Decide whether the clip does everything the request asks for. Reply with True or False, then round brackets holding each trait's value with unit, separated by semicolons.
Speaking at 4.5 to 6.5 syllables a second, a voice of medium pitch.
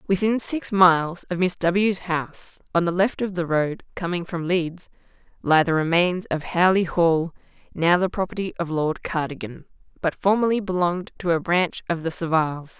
True (4.8 syllables/s; 175 Hz)